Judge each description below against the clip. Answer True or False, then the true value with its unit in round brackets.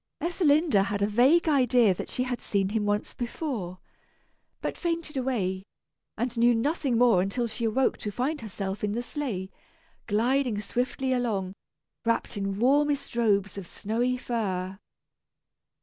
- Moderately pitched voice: False (235 Hz)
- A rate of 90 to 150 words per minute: True (145 wpm)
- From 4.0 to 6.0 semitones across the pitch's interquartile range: True (4.5 semitones)